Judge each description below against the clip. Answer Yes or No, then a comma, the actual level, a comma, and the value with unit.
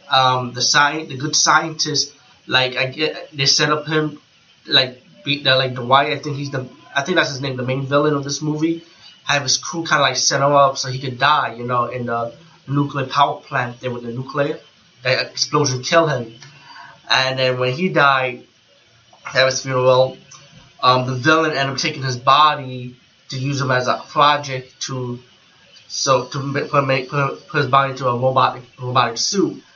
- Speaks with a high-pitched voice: No, low, 135 Hz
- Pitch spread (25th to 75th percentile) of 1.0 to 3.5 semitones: Yes, narrow, 2.5 semitones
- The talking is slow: No, average, 200 wpm